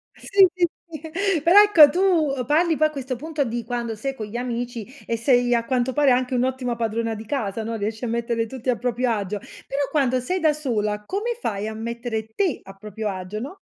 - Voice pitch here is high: Yes, high, 245 Hz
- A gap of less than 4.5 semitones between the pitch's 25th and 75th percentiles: No, average, 4.8 semitones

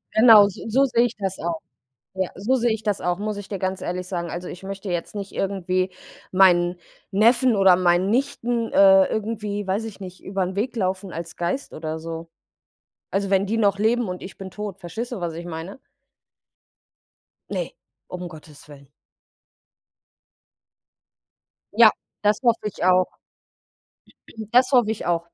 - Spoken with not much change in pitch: No, average, 3.4 semitones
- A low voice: No, high, 195 Hz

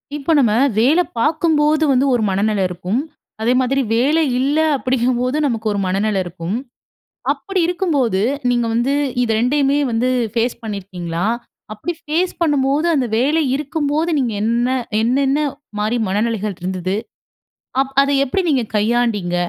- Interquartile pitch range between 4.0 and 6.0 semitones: Yes, average, 5.1 semitones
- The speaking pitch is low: No, high, 245 Hz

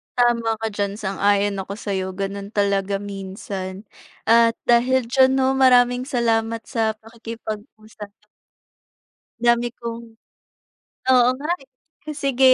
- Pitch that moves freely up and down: No, average, 3.5 semitones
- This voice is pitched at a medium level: No, high, 225 Hz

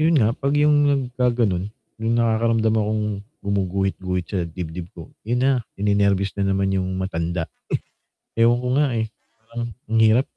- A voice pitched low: Yes, low, 105 Hz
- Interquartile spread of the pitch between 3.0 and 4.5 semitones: Yes, average, 3.6 semitones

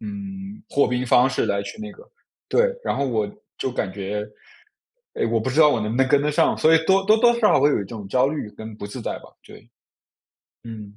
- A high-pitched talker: No, low, 130 Hz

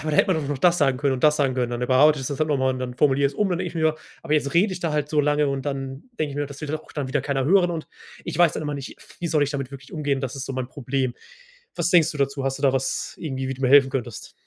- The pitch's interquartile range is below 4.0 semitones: Yes, narrow, 2.5 semitones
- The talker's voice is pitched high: No, medium, 140 Hz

